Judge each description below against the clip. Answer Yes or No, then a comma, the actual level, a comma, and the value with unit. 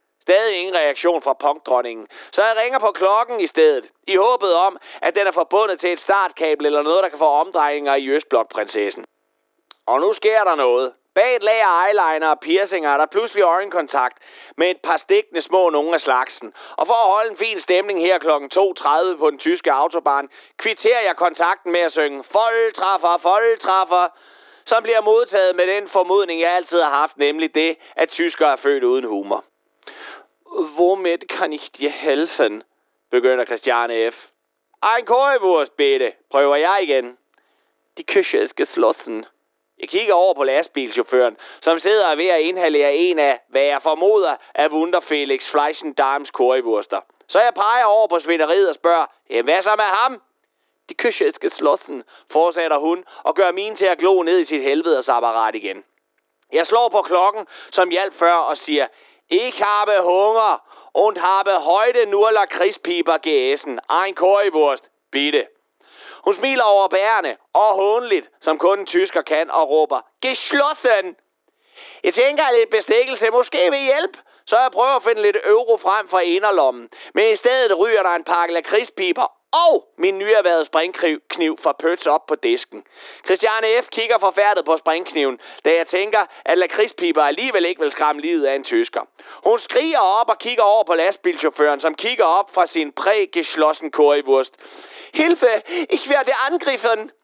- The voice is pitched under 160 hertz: No, high, 195 Hz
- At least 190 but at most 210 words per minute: No, average, 165 wpm